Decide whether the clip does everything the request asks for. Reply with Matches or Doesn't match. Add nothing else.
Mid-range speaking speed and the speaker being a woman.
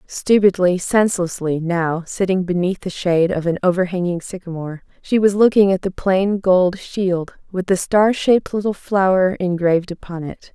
Matches